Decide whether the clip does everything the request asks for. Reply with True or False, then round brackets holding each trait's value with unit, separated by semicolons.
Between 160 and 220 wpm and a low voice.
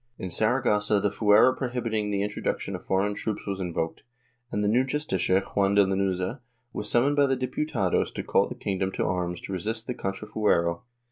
True (190 wpm; 105 Hz)